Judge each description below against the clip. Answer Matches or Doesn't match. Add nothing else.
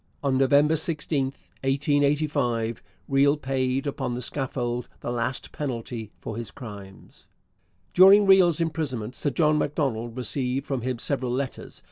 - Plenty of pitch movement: Doesn't match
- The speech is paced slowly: Matches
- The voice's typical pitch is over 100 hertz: Matches